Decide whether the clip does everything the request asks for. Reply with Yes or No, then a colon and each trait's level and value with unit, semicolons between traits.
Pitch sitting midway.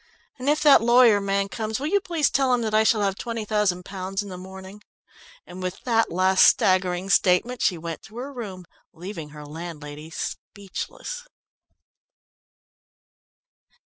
No: high, 200 Hz